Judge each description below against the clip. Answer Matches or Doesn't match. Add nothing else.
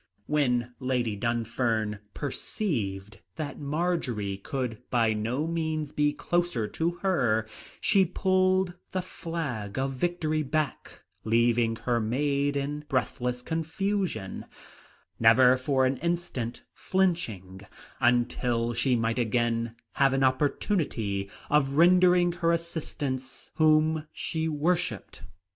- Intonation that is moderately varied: Doesn't match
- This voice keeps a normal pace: Doesn't match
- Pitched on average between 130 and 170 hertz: Matches